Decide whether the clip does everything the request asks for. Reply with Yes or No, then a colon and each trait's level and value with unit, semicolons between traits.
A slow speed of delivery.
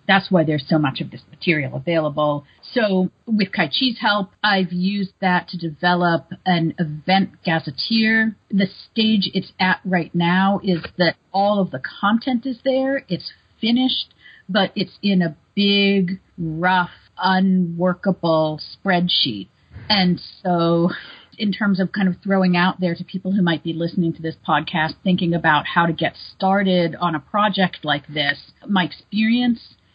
No: average, 155 wpm